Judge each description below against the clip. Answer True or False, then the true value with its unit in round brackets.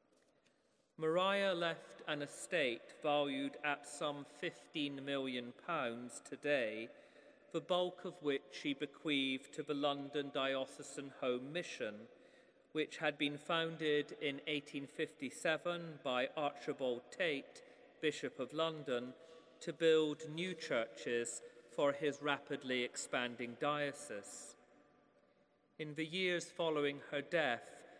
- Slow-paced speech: True (105 wpm)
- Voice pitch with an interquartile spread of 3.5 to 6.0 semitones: False (2.5 semitones)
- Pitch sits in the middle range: True (145 Hz)